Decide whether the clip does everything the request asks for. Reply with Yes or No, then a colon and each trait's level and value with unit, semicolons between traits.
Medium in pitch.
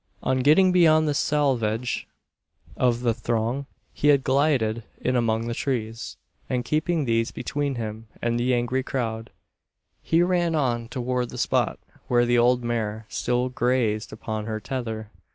No: low, 120 Hz